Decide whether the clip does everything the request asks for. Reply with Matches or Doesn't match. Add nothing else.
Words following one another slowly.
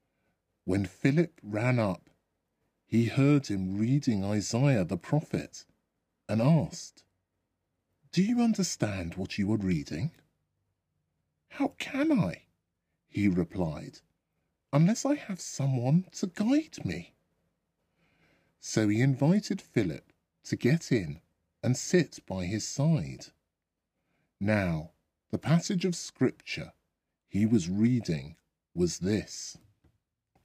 Matches